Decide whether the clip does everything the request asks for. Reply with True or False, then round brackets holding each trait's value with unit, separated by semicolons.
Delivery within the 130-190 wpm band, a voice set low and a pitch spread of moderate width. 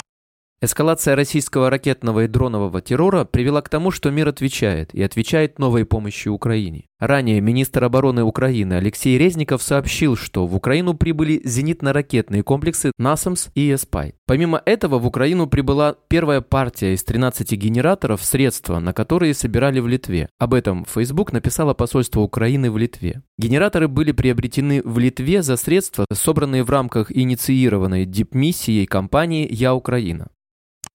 True (140 wpm; 130 Hz; 4.6 semitones)